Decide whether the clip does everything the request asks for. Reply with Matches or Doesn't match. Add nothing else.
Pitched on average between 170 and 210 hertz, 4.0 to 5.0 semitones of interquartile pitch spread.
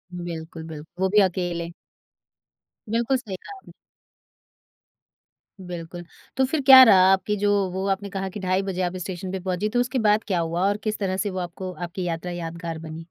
Doesn't match